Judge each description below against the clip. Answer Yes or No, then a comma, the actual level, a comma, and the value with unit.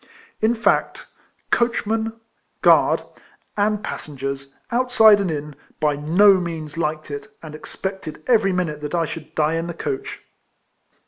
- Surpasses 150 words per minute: No, slow, 135 wpm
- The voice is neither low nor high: Yes, medium, 170 Hz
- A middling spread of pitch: No, wide, 6.1 semitones